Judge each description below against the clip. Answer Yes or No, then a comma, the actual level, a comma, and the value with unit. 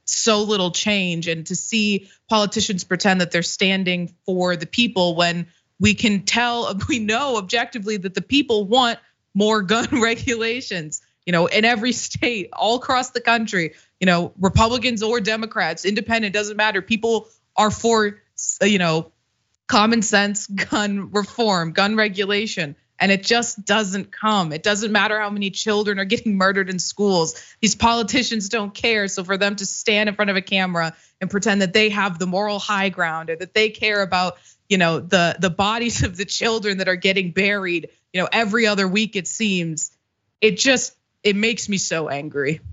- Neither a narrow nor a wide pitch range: Yes, average, 3.1 semitones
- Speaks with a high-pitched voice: Yes, high, 200 Hz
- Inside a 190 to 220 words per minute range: No, average, 175 wpm